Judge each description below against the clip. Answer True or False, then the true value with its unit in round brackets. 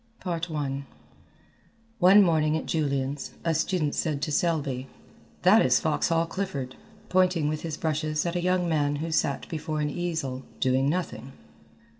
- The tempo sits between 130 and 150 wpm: True (145 wpm)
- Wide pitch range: False (3.0 semitones)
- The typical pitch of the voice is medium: True (155 Hz)